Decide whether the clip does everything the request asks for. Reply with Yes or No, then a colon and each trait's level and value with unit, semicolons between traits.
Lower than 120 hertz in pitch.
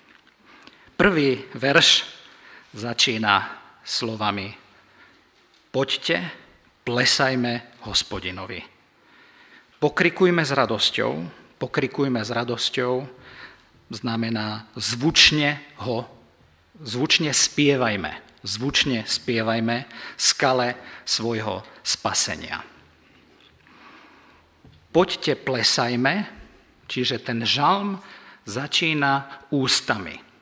No: low, 125 Hz